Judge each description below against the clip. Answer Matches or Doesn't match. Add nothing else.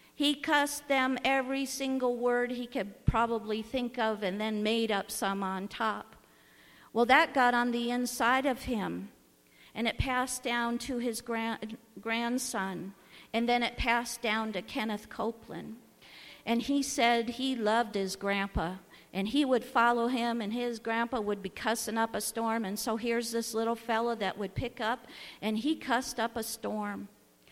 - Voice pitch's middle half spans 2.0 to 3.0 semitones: Matches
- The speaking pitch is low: Doesn't match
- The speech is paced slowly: Doesn't match